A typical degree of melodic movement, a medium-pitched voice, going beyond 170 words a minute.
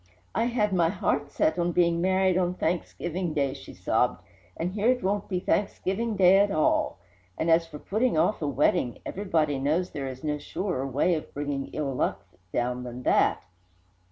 Yes: average, 4.6 semitones; medium, 170 Hz; average, 185 wpm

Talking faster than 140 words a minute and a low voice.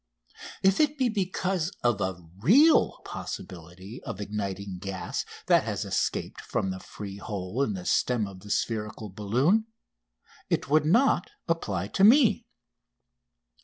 No: slow, 135 wpm; low, 110 Hz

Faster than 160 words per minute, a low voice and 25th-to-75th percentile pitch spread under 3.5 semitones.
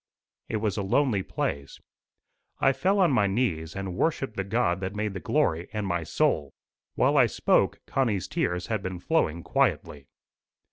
No: average, 170 wpm; low, 100 Hz; average, 4.9 semitones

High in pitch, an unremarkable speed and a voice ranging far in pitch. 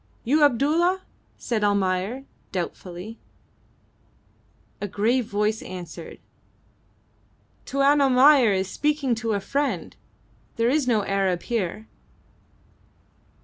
No: high, 225 Hz; slow, 95 wpm; wide, 5.8 semitones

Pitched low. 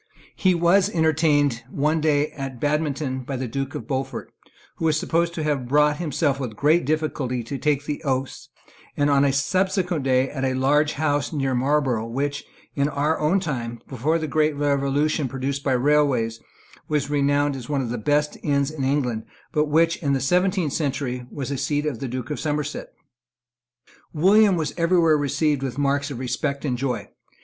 No: medium, 145 Hz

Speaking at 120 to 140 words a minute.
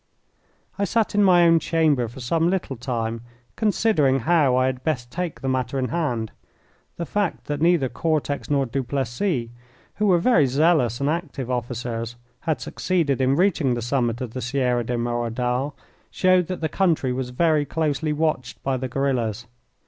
No: average, 170 wpm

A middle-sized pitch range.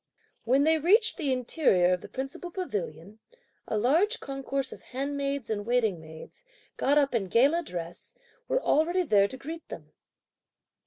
No: wide, 7.2 semitones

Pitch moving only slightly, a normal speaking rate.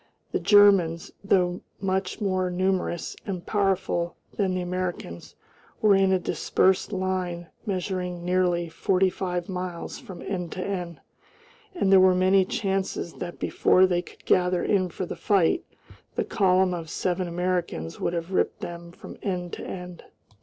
Yes: narrow, 1.5 semitones; average, 155 wpm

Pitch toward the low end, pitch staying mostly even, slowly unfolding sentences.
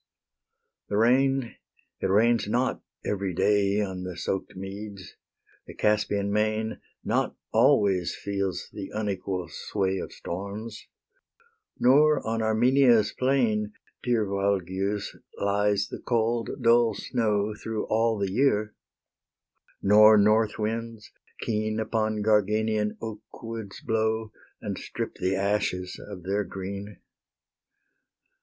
Yes: low, 105 Hz; narrow, 2.1 semitones; slow, 110 wpm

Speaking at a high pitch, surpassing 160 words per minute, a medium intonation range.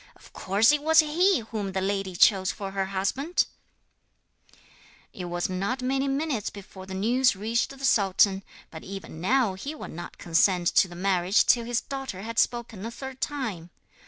No: high, 205 Hz; average, 175 wpm; wide, 5.7 semitones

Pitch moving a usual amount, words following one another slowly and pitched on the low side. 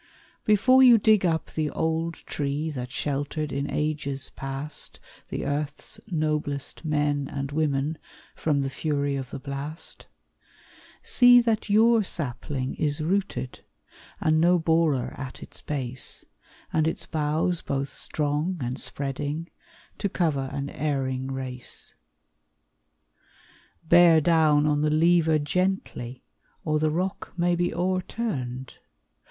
No: average, 3.3 semitones; slow, 125 wpm; medium, 150 Hz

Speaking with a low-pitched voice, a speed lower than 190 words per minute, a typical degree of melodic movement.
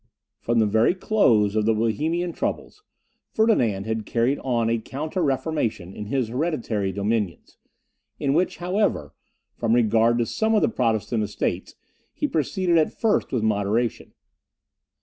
No: low, 115 Hz; average, 145 wpm; wide, 6.5 semitones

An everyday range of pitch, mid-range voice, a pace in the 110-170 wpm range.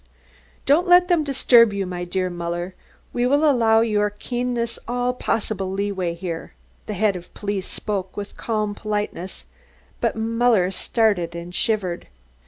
No: average, 4.3 semitones; high, 210 Hz; average, 145 wpm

